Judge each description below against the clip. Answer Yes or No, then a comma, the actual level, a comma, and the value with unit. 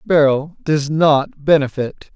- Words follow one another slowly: Yes, slow, 110 wpm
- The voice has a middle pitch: Yes, medium, 145 Hz